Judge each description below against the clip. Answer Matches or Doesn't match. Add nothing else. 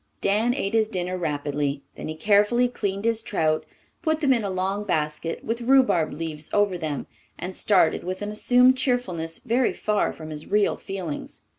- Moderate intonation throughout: Doesn't match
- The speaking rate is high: Doesn't match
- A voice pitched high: Matches